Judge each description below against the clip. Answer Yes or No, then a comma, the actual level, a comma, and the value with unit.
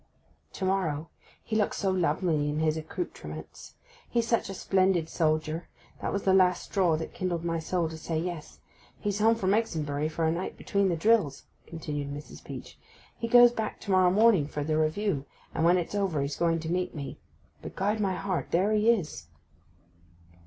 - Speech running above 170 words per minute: Yes, average, 190 wpm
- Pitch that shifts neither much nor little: Yes, average, 4.0 semitones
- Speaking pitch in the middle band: Yes, medium, 175 Hz